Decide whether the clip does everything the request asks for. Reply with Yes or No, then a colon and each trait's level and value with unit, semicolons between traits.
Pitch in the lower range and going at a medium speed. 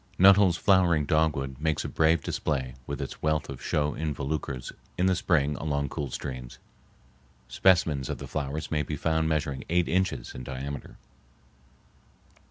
Yes: very low, 75 Hz; average, 150 wpm